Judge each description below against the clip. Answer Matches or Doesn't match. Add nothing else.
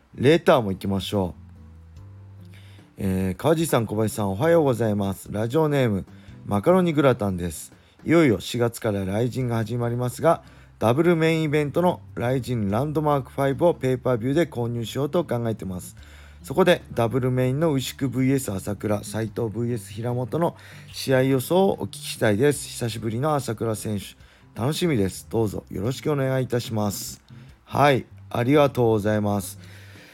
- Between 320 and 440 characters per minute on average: Matches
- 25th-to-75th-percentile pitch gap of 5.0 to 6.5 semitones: Matches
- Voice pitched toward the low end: Matches